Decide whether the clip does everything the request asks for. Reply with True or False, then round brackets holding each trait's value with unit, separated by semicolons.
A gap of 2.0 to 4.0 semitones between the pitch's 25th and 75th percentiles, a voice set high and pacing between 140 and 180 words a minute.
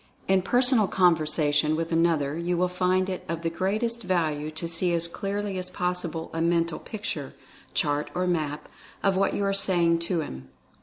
False (2.5 semitones; 170 Hz; 175 wpm)